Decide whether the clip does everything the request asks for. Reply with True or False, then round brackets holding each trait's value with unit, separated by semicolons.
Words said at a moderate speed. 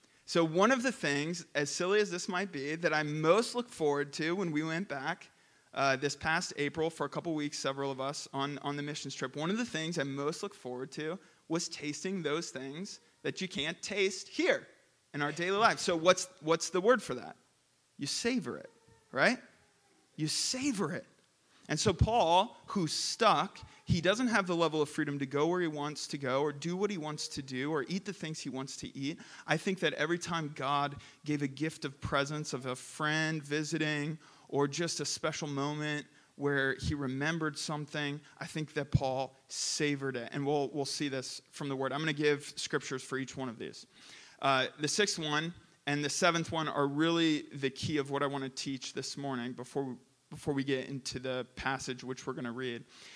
False (210 wpm)